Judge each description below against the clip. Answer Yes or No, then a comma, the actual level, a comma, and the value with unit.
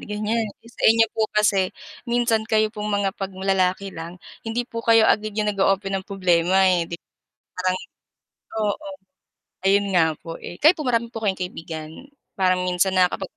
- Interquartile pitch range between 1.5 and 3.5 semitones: Yes, average, 3.1 semitones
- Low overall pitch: No, high, 195 Hz